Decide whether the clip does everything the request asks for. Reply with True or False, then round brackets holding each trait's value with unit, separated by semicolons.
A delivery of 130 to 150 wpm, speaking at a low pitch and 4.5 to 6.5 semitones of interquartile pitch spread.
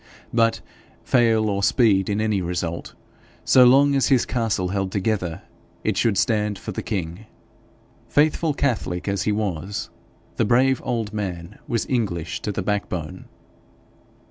False (145 wpm; 105 Hz; 3.8 semitones)